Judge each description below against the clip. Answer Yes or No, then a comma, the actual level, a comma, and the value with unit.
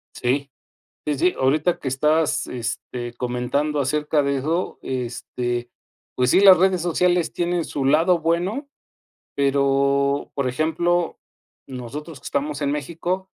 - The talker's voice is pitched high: No, medium, 145 Hz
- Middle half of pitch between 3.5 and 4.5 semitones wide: Yes, average, 4.2 semitones